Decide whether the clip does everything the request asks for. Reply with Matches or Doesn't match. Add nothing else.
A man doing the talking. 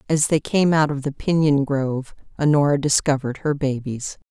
Doesn't match